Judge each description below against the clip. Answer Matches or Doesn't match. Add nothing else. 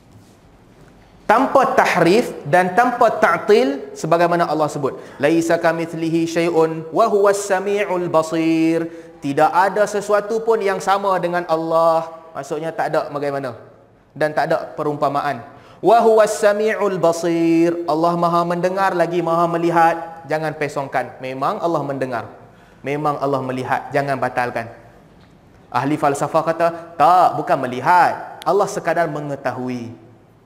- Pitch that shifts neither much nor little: Matches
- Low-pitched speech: Doesn't match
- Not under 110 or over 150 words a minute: Matches